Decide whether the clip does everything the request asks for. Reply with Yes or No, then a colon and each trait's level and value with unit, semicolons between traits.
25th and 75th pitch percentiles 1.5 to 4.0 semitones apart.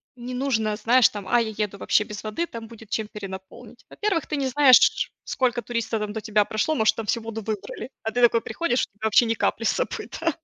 Yes: narrow, 2.6 semitones